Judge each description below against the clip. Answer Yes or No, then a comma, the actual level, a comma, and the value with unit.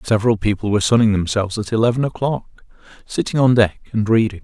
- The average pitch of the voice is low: Yes, low, 110 Hz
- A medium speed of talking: Yes, average, 175 wpm